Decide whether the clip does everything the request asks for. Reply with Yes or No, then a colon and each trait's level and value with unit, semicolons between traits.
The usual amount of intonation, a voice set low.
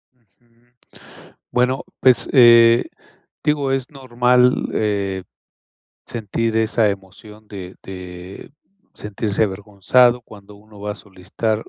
Yes: average, 3.5 semitones; low, 110 Hz